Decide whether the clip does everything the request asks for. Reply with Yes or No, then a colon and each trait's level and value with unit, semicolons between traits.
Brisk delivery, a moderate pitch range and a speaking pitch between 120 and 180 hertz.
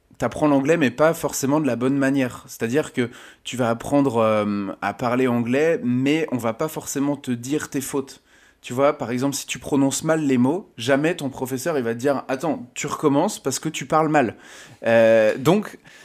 Yes: fast, 200 wpm; average, 3.0 semitones; low, 135 Hz